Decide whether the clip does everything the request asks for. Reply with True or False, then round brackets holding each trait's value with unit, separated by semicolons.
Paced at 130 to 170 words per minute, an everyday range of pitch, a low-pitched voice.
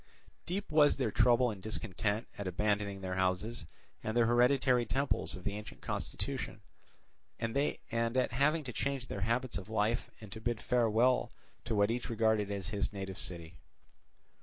True (160 wpm; 3.4 semitones; 110 Hz)